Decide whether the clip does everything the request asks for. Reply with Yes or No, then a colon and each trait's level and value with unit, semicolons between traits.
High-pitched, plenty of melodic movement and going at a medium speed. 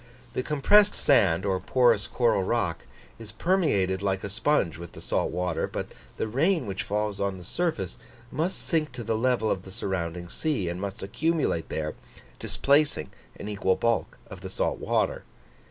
No: low, 105 Hz; wide, 7.0 semitones; average, 170 wpm